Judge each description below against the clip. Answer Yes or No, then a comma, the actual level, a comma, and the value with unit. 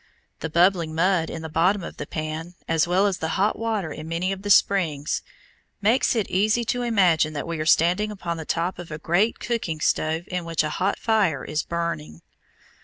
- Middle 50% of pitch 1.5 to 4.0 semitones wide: Yes, average, 3.7 semitones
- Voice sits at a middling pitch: Yes, medium, 170 Hz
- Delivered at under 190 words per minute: No, fast, 205 wpm